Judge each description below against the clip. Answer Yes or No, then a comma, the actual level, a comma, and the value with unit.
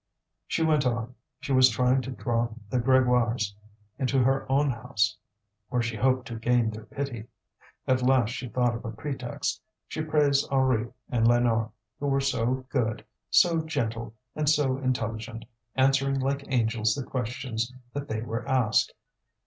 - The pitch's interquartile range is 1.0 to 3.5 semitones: Yes, average, 2.8 semitones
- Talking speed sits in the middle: Yes, average, 155 wpm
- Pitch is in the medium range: No, low, 125 Hz